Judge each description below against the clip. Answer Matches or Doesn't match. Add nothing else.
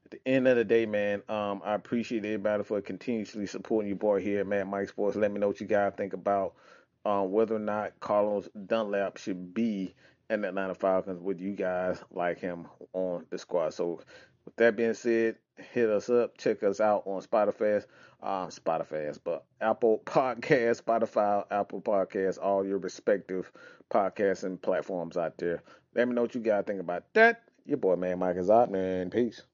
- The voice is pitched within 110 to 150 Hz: Doesn't match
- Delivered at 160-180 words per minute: Doesn't match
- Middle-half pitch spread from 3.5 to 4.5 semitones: Doesn't match